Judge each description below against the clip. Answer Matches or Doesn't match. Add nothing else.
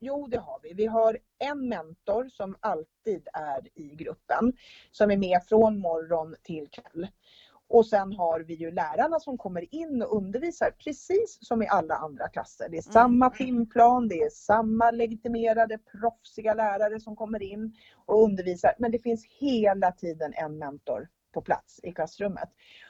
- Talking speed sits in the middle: Matches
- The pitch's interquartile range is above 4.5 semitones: Matches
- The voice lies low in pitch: Doesn't match